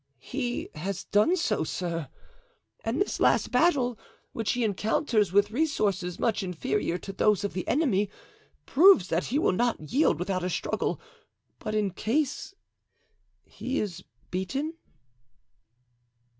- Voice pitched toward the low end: No, high, 210 Hz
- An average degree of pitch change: No, wide, 5.9 semitones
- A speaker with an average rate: No, slow, 130 wpm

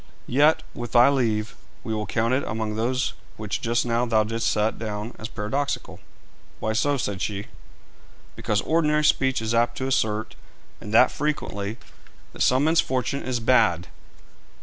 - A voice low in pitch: Yes, low, 115 Hz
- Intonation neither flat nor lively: Yes, average, 3.4 semitones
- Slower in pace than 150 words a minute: No, average, 165 wpm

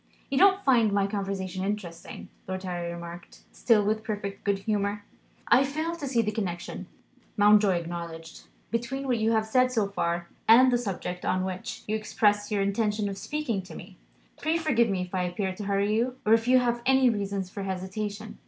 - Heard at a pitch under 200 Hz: No, high, 205 Hz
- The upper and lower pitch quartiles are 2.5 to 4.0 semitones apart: Yes, average, 3.6 semitones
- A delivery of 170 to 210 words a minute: Yes, average, 190 wpm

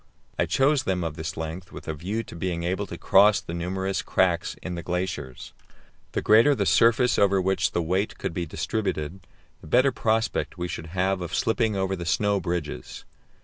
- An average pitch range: Yes, average, 3.3 semitones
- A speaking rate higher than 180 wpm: Yes, average, 190 wpm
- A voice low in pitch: Yes, very low, 95 Hz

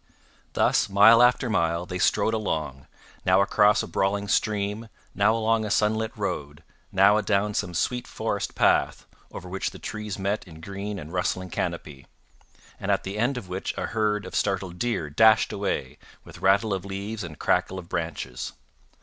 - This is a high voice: No, low, 100 Hz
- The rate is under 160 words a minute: No, average, 170 wpm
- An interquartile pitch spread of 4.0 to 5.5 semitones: No, average, 3.1 semitones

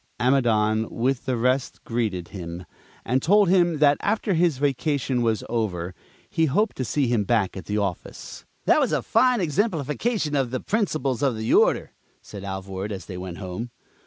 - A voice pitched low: Yes, low, 125 Hz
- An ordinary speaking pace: Yes, average, 175 wpm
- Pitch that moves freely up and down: Yes, wide, 6.6 semitones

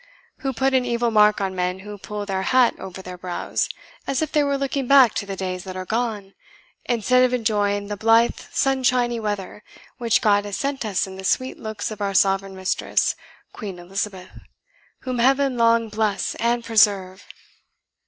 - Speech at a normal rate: Yes, average, 180 wpm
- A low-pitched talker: No, high, 215 Hz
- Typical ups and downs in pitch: Yes, average, 3.9 semitones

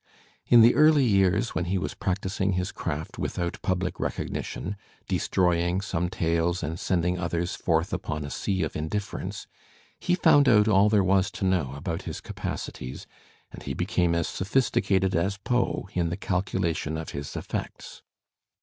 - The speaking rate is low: No, average, 165 wpm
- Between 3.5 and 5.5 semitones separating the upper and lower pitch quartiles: No, average, 2.8 semitones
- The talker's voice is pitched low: Yes, very low, 90 Hz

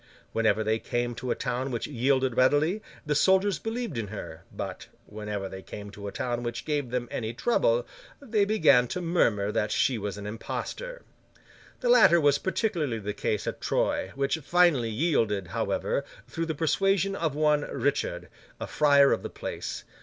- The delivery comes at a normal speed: Yes, average, 175 wpm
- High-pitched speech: No, low, 135 Hz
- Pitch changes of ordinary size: No, wide, 7.4 semitones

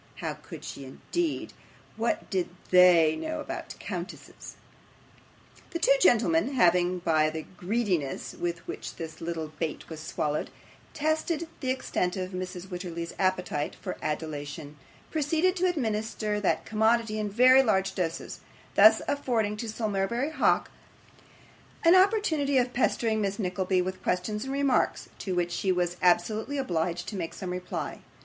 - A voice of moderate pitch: No, high, 195 Hz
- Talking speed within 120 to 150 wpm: Yes, average, 145 wpm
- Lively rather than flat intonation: Yes, wide, 6.5 semitones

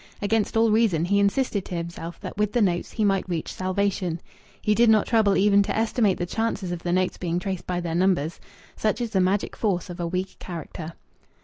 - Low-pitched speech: No, high, 190 Hz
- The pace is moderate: No, fast, 215 wpm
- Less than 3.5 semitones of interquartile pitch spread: Yes, average, 3.1 semitones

